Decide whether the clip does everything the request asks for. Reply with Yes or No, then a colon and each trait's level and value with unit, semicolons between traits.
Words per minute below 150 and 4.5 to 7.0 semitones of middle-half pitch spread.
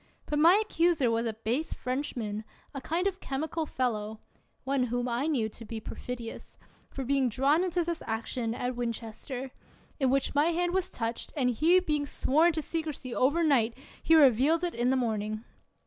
No: average, 180 wpm; average, 5.2 semitones